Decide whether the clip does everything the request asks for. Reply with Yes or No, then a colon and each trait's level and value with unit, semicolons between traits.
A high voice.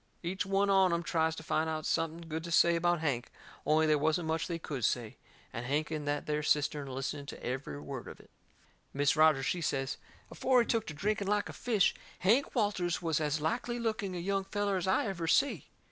No: medium, 165 Hz